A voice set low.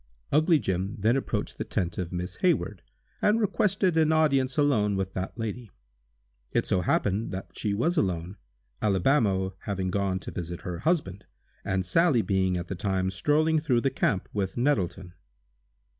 Yes: low, 100 Hz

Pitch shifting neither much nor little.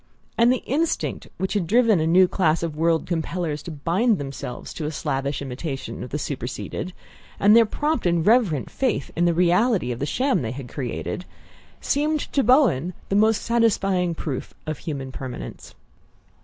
No: wide, 7.6 semitones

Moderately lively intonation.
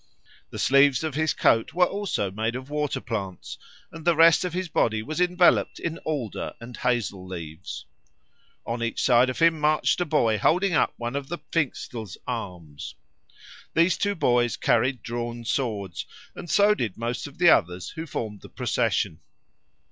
No: wide, 6.5 semitones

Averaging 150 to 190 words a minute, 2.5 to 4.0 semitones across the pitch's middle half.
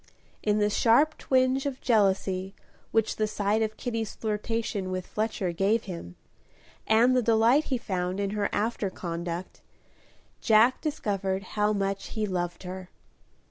No: average, 140 wpm; average, 3.2 semitones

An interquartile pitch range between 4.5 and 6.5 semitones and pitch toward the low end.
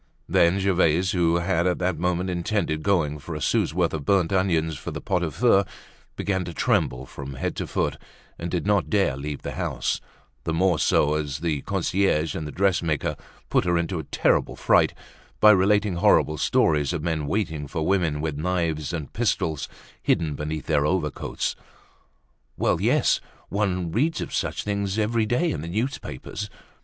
No: average, 4.0 semitones; very low, 85 Hz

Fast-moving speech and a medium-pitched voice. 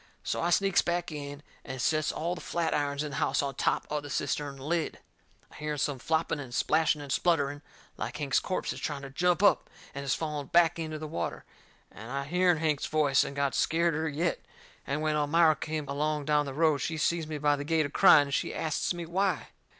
Yes: fast, 220 wpm; medium, 150 Hz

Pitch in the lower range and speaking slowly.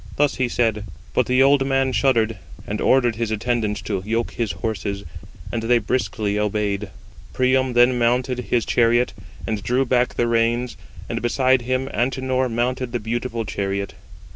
No: low, 120 Hz; average, 160 wpm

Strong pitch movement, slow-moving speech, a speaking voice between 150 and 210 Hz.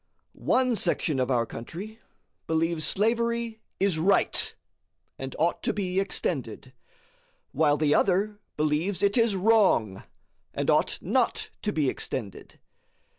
Yes: wide, 5.8 semitones; slow, 125 wpm; medium, 185 Hz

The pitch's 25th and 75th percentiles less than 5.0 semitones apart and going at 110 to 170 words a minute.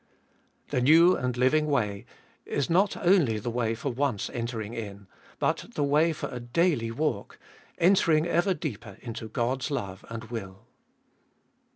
No: average, 5.3 semitones; average, 155 wpm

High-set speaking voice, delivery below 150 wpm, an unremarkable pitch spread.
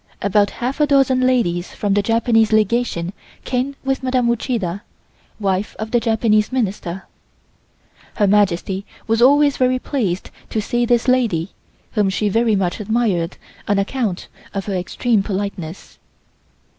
Yes: high, 215 Hz; average, 140 wpm; average, 3.9 semitones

